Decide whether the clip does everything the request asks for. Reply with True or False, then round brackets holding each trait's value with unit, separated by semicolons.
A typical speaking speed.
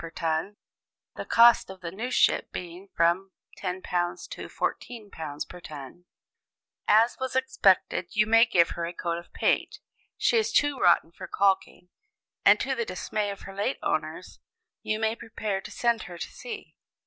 True (170 wpm)